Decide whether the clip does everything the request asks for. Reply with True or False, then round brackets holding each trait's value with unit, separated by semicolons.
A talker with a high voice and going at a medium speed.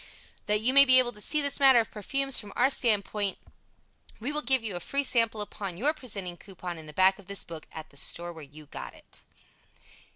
False (210 Hz; 225 wpm)